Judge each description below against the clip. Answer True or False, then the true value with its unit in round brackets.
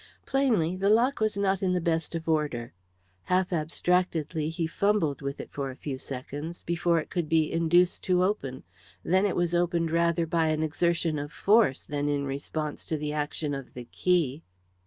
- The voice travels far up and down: False (3.3 semitones)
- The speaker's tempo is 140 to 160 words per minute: False (180 wpm)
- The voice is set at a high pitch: False (165 Hz)